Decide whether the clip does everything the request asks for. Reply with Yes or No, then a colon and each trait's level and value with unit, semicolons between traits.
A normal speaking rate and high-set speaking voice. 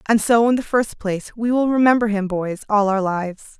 No: fast, 235 wpm; high, 215 Hz